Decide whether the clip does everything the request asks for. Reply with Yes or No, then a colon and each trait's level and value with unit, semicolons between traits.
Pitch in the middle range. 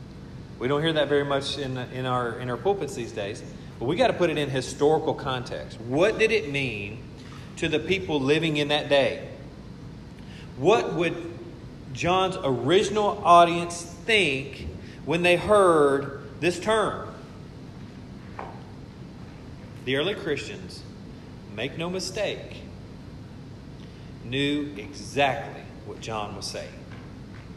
Yes: medium, 145 Hz